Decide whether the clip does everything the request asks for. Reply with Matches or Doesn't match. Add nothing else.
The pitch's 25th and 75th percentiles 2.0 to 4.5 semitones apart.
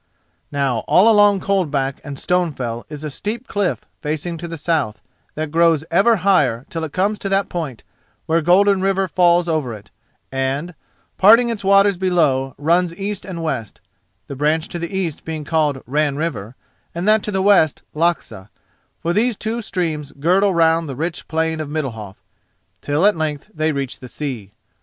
Doesn't match